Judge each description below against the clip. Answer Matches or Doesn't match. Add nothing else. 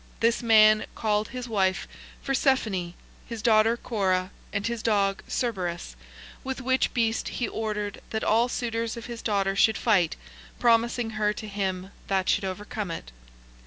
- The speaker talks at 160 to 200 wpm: Doesn't match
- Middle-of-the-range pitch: Doesn't match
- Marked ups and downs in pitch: Doesn't match